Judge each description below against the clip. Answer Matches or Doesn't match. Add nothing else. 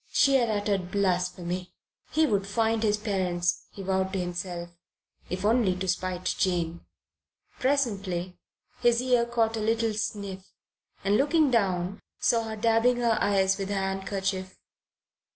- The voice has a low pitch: Doesn't match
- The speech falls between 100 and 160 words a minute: Matches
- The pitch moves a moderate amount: Matches